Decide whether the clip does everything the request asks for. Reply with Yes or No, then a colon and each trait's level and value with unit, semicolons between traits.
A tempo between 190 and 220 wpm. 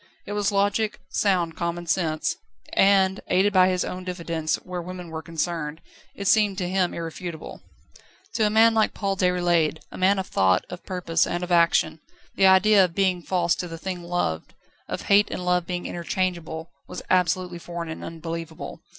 No: average, 175 wpm